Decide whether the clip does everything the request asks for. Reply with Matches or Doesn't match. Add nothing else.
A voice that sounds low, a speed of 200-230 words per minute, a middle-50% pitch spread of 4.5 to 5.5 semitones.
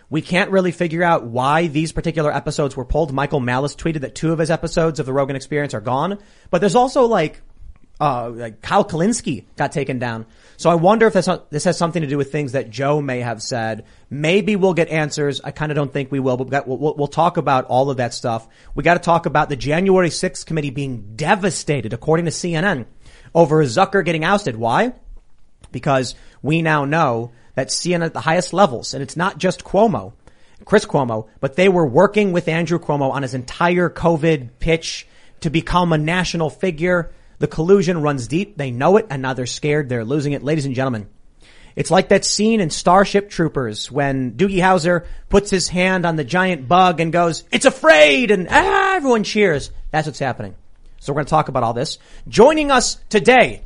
Doesn't match